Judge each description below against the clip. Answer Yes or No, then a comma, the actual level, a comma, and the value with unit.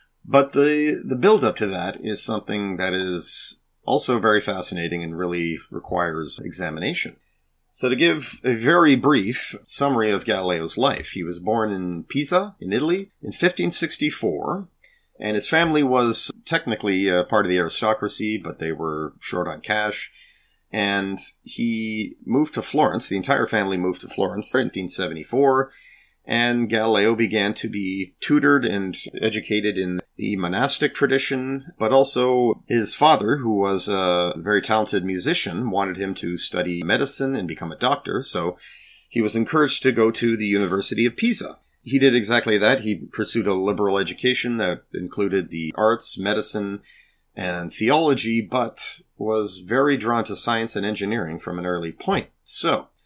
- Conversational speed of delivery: Yes, average, 155 wpm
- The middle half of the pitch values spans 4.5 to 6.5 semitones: Yes, average, 4.8 semitones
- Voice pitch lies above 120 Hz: No, low, 110 Hz